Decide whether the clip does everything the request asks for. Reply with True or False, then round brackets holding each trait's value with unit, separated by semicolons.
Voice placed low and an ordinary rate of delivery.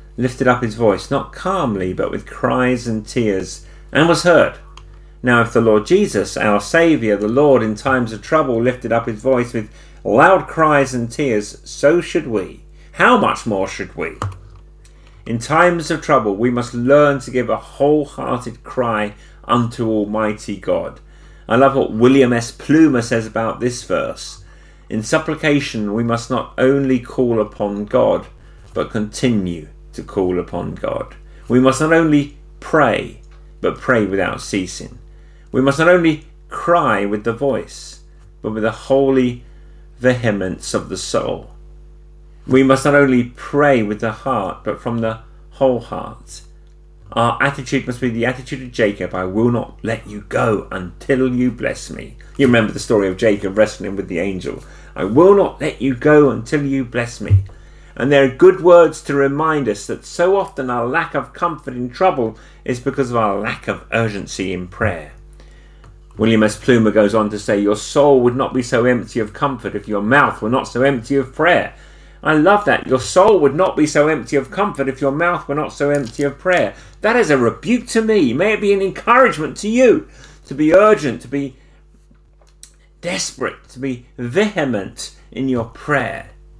True (125 Hz; 180 wpm)